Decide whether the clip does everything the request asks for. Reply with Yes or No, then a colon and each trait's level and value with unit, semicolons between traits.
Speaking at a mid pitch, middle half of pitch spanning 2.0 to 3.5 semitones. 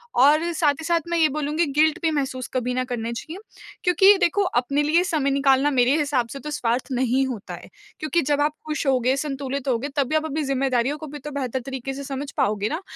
No: very high, 280 Hz; average, 3.0 semitones